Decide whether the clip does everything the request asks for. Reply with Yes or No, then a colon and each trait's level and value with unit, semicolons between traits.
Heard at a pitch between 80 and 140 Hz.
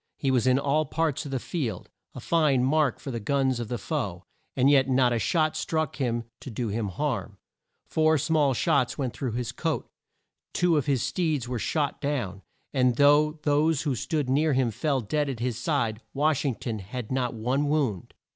Yes: low, 135 Hz